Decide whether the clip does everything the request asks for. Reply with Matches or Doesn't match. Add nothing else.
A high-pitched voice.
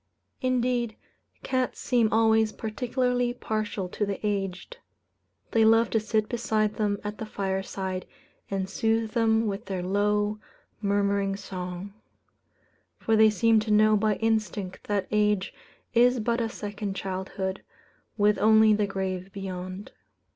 Matches